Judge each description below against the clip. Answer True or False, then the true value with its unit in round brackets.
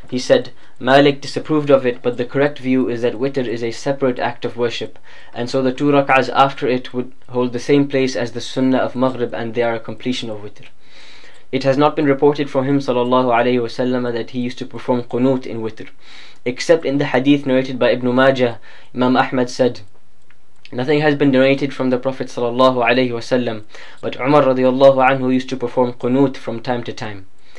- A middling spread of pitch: False (1.8 semitones)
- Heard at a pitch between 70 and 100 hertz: False (125 Hz)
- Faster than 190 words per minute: True (200 wpm)